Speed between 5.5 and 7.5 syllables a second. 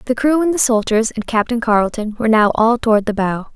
Yes: 5.9 syllables/s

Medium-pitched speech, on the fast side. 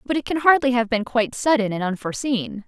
No: high, 240 Hz; fast, 225 wpm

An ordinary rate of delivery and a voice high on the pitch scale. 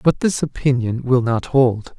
No: average, 180 wpm; low, 130 Hz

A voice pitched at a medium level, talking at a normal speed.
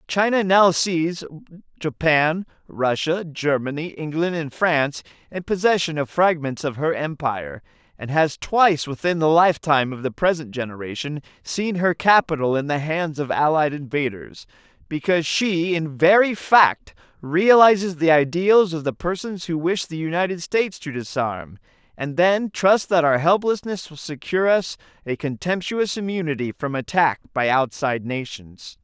Yes: medium, 160 Hz; average, 145 wpm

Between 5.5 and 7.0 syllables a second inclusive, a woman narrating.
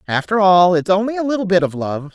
Yes: 6.0 syllables/s; female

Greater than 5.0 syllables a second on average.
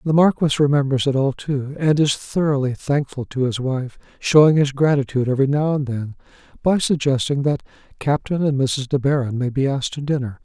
Yes: 5.6 syllables/s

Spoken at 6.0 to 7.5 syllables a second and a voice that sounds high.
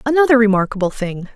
Yes: 6.8 syllables/s; high, 225 Hz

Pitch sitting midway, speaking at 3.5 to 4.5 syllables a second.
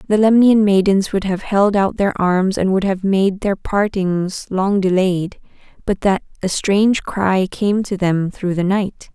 No: high, 195 Hz; 4.0 syllables/s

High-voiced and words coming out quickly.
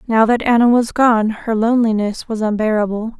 No: high, 225 Hz; average, 170 wpm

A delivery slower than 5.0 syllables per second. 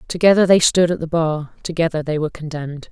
No: 6.3 syllables/s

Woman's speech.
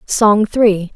Yes: female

